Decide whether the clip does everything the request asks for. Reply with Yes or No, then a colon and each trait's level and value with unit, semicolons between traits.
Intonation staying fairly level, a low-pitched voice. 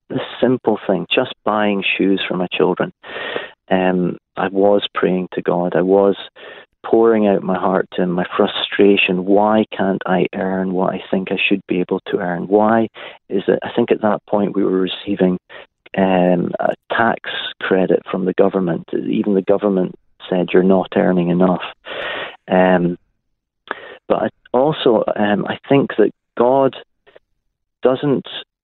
Yes: narrow, 1.9 semitones; very low, 95 Hz